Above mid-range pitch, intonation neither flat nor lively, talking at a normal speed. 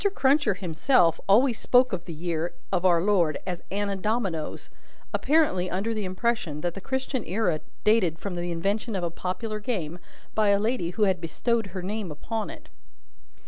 Yes: high, 195 Hz; average, 4.3 semitones; average, 175 wpm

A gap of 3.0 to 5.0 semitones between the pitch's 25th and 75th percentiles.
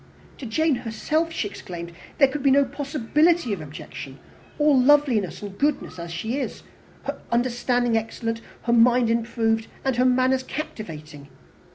Yes: average, 3.9 semitones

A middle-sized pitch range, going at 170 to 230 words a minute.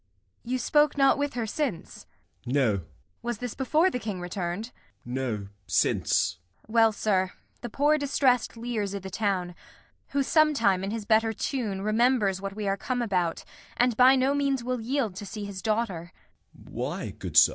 Yes: average, 5.0 semitones; average, 185 wpm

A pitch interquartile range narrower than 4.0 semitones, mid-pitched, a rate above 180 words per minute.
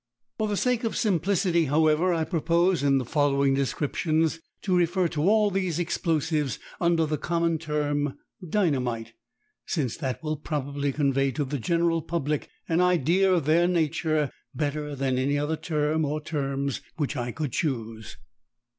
No: average, 3.2 semitones; medium, 155 Hz; average, 155 wpm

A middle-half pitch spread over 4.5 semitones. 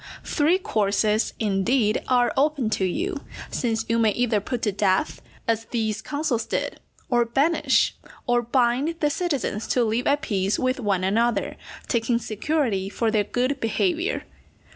No: average, 4.1 semitones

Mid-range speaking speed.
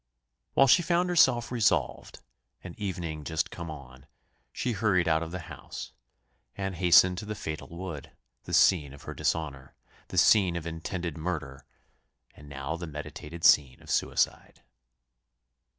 Yes: average, 150 wpm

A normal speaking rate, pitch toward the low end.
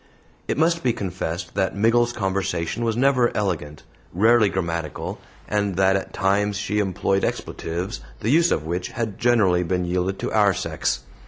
Yes: average, 160 wpm; very low, 95 Hz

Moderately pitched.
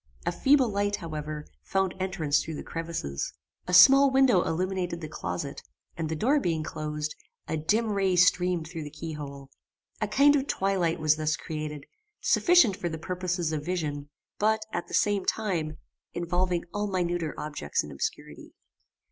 Yes: medium, 175 Hz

